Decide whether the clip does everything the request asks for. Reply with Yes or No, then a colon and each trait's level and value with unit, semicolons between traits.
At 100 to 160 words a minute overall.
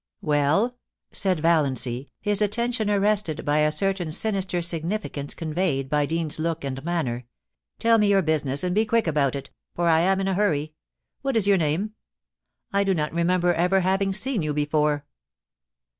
No: average, 175 wpm